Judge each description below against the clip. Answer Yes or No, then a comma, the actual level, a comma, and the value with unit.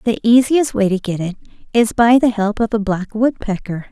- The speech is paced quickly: Yes, fast, 215 wpm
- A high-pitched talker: Yes, high, 220 Hz